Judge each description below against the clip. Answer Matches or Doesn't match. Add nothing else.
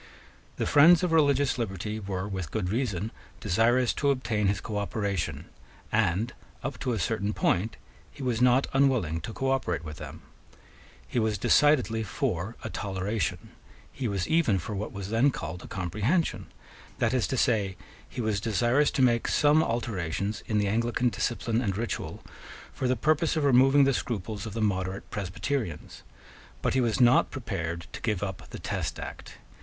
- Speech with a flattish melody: Doesn't match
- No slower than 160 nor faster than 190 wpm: Matches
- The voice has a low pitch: Matches